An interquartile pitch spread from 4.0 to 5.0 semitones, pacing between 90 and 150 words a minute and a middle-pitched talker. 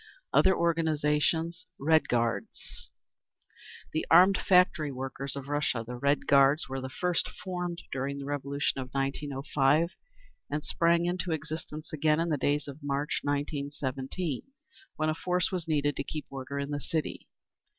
No: average, 3.0 semitones; average, 145 wpm; medium, 150 Hz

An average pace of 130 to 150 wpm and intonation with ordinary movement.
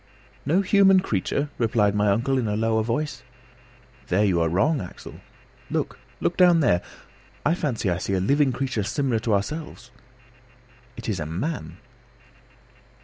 No: average, 145 wpm; wide, 6.8 semitones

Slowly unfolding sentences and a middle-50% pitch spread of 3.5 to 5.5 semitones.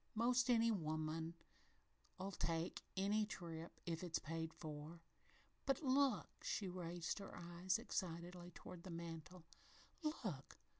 Yes: slow, 115 wpm; average, 4.1 semitones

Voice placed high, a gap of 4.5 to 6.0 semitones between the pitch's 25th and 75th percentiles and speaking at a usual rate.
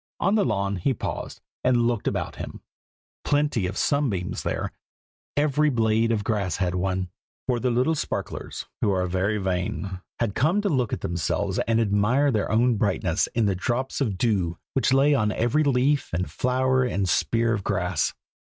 No: low, 115 Hz; average, 5.2 semitones; average, 175 wpm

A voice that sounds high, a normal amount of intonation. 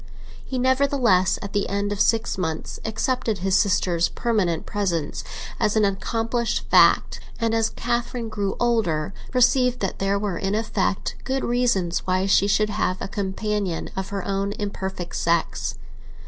Yes: high, 205 Hz; average, 3.2 semitones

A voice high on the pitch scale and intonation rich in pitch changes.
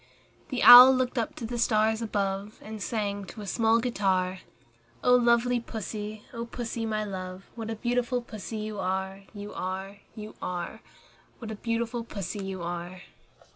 No: high, 215 Hz; average, 3.3 semitones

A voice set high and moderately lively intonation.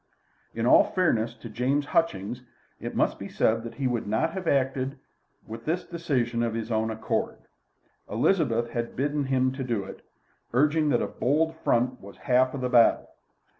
No: low, 125 Hz; average, 3.8 semitones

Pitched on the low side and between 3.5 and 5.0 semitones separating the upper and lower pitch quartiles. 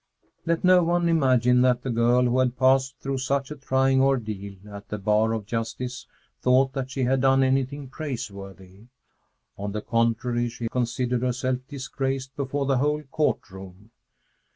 No: low, 130 Hz; narrow, 2.6 semitones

